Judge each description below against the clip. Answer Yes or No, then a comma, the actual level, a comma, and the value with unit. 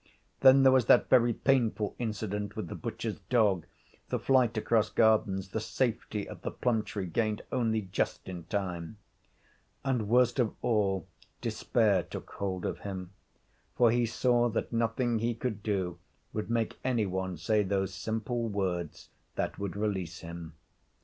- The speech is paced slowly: No, average, 155 wpm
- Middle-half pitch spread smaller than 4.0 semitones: Yes, average, 3.5 semitones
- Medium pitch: No, low, 110 Hz